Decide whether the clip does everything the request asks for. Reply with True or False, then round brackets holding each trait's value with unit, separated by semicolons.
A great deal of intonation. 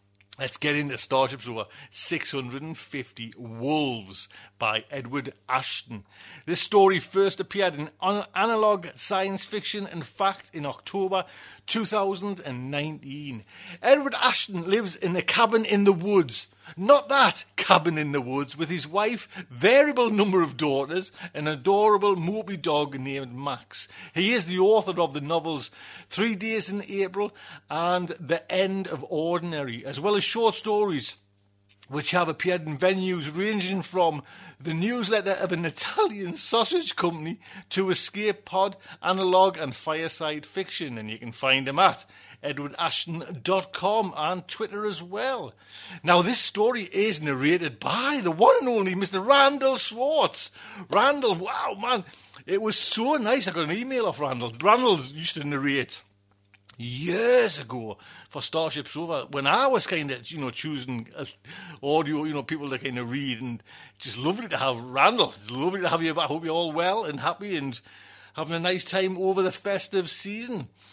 True (5.9 semitones)